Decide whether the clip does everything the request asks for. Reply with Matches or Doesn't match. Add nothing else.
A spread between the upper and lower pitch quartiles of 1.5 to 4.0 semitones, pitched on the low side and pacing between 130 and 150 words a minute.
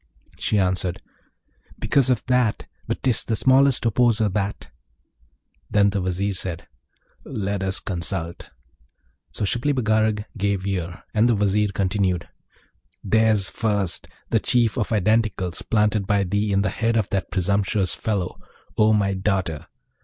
Matches